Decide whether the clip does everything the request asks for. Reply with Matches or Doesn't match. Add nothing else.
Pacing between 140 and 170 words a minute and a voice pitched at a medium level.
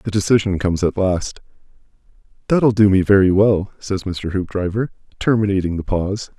Doesn't match